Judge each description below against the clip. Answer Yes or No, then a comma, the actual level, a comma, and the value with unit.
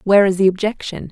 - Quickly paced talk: Yes, fast, 215 wpm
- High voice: Yes, high, 195 Hz